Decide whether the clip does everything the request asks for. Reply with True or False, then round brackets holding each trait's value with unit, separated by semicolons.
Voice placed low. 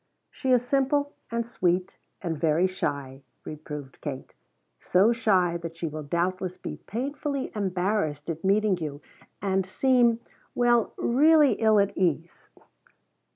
False (190 Hz)